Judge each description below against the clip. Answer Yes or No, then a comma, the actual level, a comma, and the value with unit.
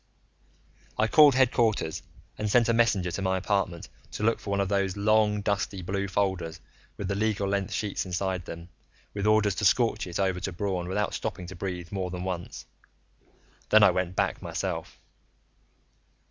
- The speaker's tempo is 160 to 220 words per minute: Yes, average, 175 wpm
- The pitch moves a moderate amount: No, narrow, 2.3 semitones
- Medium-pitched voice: No, low, 100 Hz